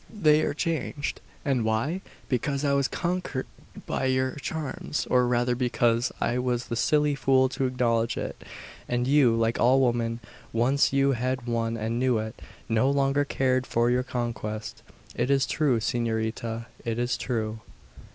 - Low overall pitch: Yes, low, 125 Hz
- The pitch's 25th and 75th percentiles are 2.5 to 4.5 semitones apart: Yes, average, 2.8 semitones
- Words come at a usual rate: Yes, average, 160 wpm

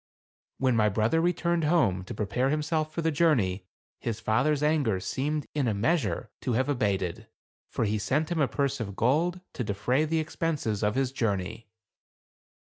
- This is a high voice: No, low, 130 Hz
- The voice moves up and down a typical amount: No, wide, 6.4 semitones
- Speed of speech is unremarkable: Yes, average, 170 wpm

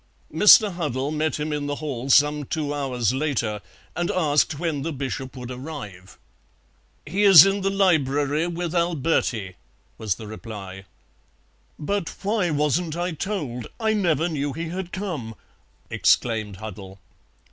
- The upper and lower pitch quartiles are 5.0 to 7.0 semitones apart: Yes, wide, 5.6 semitones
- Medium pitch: Yes, medium, 150 Hz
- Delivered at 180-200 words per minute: No, average, 140 wpm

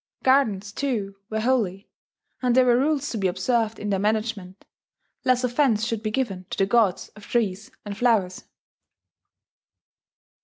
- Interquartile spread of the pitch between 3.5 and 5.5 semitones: Yes, average, 3.9 semitones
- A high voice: Yes, high, 220 Hz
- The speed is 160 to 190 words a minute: No, average, 150 wpm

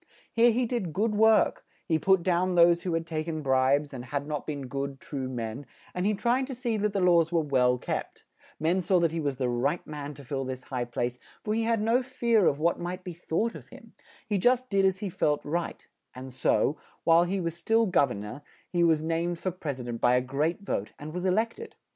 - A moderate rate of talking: No, fast, 245 wpm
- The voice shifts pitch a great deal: Yes, wide, 5.8 semitones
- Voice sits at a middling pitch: Yes, medium, 165 Hz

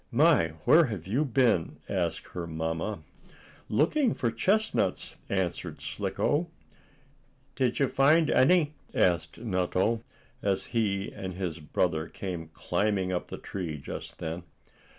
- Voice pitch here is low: Yes, low, 100 Hz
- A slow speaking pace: Yes, slow, 125 wpm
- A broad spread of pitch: Yes, wide, 7.6 semitones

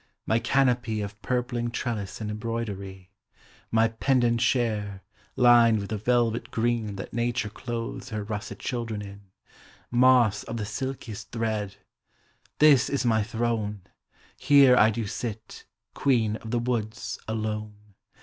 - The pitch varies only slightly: Yes, narrow, 2.3 semitones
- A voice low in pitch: Yes, low, 115 Hz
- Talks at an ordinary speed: No, slow, 130 wpm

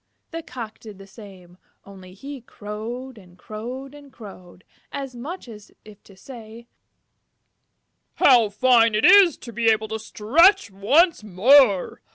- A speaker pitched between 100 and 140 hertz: No, high, 225 Hz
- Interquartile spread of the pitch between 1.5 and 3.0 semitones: No, average, 4.5 semitones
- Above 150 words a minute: No, average, 140 wpm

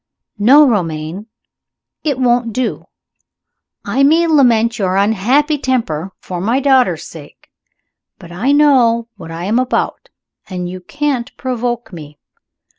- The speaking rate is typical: No, slow, 125 wpm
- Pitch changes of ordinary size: No, wide, 6.1 semitones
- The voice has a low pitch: No, high, 235 Hz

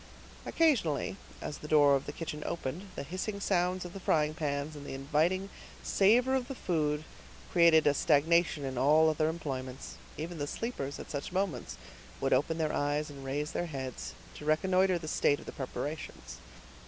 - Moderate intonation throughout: Yes, average, 3.8 semitones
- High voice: No, medium, 155 Hz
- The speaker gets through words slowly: No, average, 180 wpm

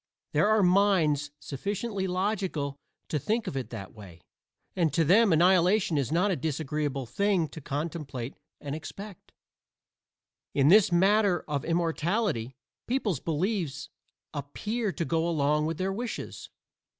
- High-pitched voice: No, medium, 170 Hz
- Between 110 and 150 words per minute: Yes, slow, 135 wpm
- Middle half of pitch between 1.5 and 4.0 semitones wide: No, average, 5.3 semitones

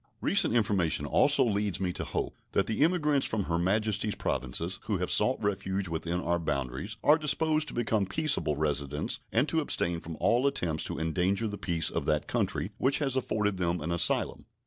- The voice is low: Yes, low, 100 Hz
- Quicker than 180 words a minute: Yes, average, 190 wpm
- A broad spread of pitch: Yes, wide, 5.7 semitones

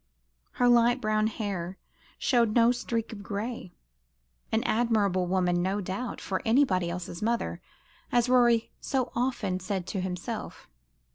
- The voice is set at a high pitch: Yes, high, 215 Hz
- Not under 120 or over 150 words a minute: Yes, slow, 135 wpm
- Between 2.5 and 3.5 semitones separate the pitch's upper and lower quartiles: No, average, 4.3 semitones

